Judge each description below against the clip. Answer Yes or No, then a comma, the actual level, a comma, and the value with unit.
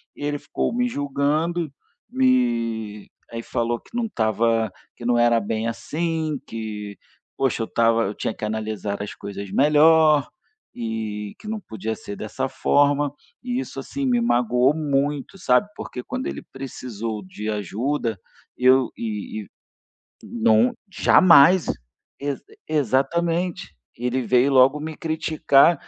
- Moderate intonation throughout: No, wide, 5.9 semitones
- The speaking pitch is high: No, low, 130 Hz